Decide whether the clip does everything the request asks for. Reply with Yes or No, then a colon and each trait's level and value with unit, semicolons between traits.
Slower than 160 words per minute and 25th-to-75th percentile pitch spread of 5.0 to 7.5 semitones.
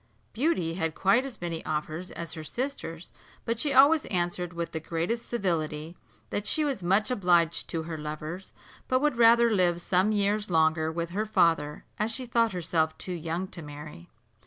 No: average, 180 wpm; wide, 5.5 semitones